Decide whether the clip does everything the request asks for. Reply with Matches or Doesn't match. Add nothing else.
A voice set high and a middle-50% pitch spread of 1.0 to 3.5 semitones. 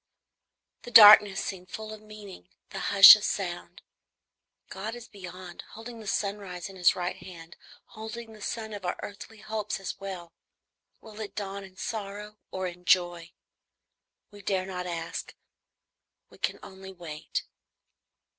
Matches